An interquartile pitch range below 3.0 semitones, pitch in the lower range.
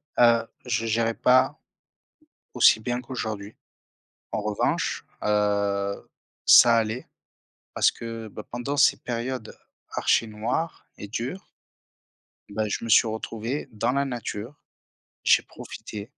Yes: narrow, 2.4 semitones; low, 115 Hz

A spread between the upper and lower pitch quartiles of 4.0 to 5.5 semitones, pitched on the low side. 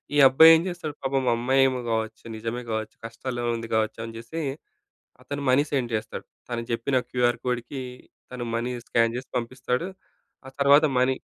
No: narrow, 2.6 semitones; low, 125 Hz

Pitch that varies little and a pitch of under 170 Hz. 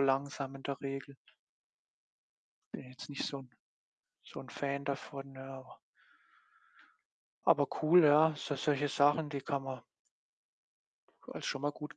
Yes: narrow, 1.3 semitones; medium, 140 Hz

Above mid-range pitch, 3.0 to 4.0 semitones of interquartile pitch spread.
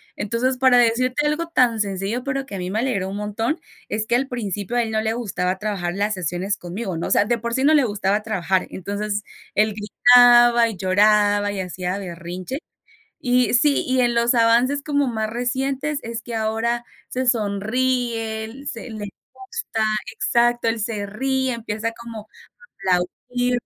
Yes: high, 225 Hz; average, 3.3 semitones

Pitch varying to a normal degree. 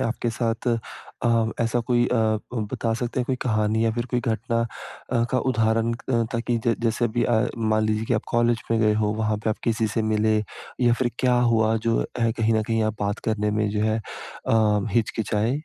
No: narrow, 1.4 semitones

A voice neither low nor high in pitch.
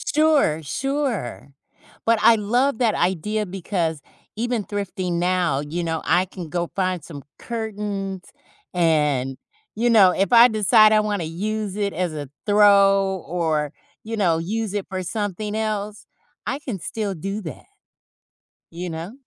No: high, 195 Hz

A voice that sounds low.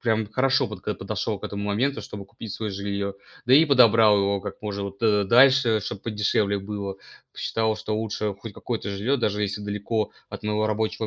Yes: low, 105 Hz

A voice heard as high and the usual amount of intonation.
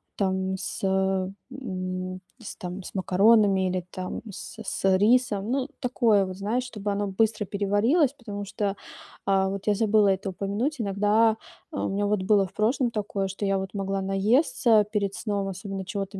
No: high, 200 Hz; narrow, 2.2 semitones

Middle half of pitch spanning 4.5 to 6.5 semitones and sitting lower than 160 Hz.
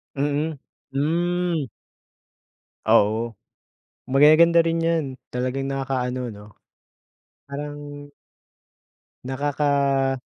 No: average, 2.9 semitones; medium, 140 Hz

